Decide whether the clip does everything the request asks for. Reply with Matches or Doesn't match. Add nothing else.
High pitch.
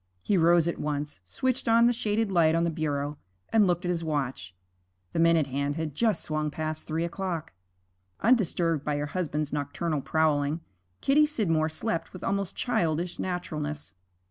Doesn't match